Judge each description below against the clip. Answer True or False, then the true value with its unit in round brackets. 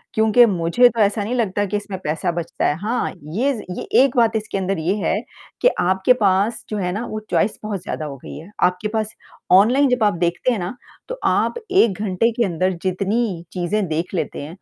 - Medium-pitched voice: False (200 Hz)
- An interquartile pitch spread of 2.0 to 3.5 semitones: False (3.9 semitones)